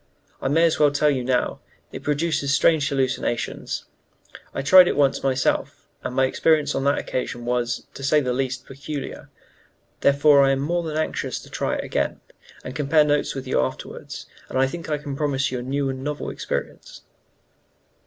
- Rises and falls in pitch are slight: Yes, narrow, 2.2 semitones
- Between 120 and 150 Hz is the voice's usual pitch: Yes, medium, 140 Hz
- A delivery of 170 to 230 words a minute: Yes, average, 185 wpm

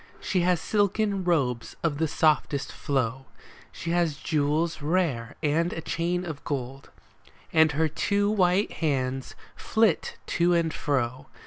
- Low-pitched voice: No, medium, 160 Hz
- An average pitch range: Yes, average, 3.9 semitones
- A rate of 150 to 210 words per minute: No, slow, 135 wpm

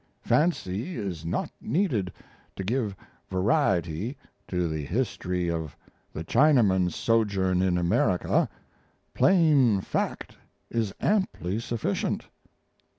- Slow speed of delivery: Yes, slow, 95 wpm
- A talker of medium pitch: No, low, 100 Hz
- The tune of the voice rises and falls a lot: Yes, wide, 6.1 semitones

